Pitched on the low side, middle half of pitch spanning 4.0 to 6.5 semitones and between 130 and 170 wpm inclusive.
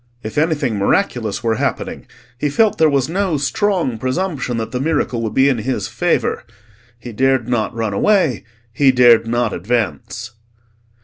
Yes: low, 125 Hz; average, 4.8 semitones; average, 160 wpm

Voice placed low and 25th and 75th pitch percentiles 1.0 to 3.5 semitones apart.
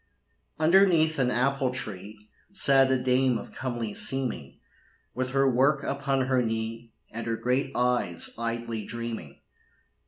Yes: low, 125 Hz; average, 2.9 semitones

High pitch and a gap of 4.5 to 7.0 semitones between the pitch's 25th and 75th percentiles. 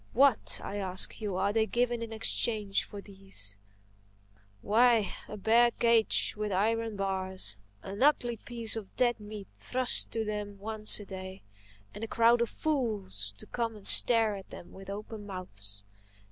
No: high, 210 Hz; average, 3.0 semitones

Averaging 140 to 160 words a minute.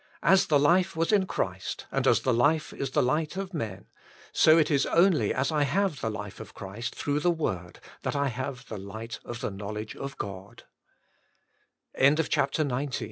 No: average, 175 wpm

